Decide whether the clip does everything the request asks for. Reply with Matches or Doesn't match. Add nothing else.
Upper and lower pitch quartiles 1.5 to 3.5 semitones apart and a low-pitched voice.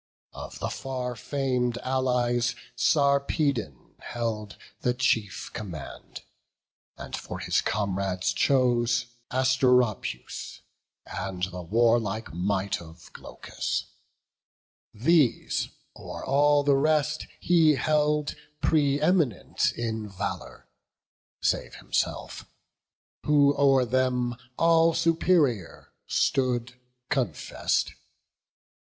Doesn't match